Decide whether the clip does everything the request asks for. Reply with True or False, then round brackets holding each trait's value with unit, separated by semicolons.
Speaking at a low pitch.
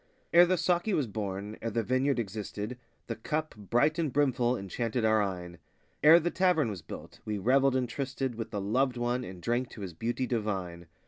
True (120 Hz)